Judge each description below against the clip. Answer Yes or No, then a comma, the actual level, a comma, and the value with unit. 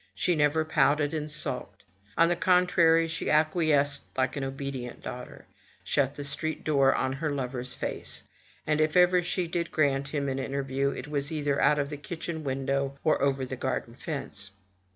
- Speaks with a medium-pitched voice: Yes, medium, 145 Hz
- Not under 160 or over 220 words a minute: Yes, average, 175 wpm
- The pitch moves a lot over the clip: No, narrow, 2.6 semitones